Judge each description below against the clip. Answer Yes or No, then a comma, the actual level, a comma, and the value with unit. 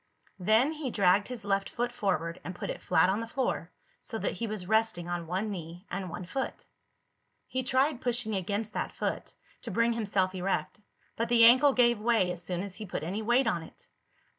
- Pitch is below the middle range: No, high, 210 Hz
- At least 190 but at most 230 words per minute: Yes, fast, 205 wpm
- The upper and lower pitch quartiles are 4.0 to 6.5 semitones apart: Yes, average, 4.5 semitones